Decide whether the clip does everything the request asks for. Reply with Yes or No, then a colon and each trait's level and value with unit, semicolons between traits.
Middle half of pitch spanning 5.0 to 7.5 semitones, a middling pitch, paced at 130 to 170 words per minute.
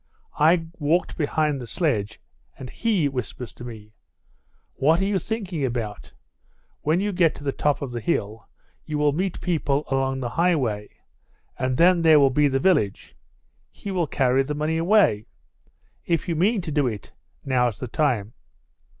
Yes: average, 5.3 semitones; medium, 145 Hz; average, 165 wpm